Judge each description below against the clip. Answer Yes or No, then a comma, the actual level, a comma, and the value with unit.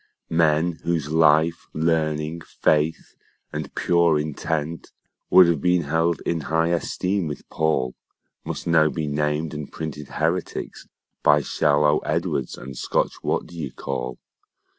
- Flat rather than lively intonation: Yes, narrow, 1.9 semitones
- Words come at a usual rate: No, slow, 130 wpm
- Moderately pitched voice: No, very low, 80 Hz